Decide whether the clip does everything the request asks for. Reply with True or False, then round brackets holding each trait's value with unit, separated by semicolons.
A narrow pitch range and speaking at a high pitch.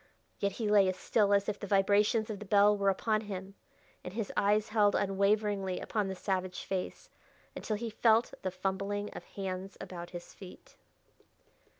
True (1.7 semitones; 200 Hz)